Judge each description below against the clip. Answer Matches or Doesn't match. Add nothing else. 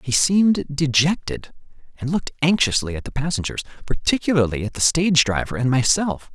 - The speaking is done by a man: Matches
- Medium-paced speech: Matches